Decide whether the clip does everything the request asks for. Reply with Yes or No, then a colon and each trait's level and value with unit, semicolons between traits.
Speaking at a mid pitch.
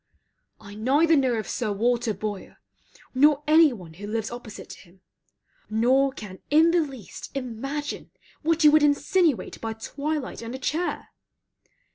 No: very high, 260 Hz